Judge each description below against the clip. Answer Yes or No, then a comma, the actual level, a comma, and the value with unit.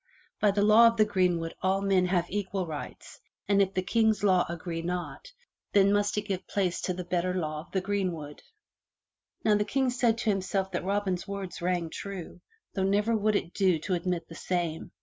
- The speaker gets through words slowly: No, average, 200 wpm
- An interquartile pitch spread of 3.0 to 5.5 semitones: No, narrow, 2.5 semitones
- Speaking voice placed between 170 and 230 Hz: Yes, high, 190 Hz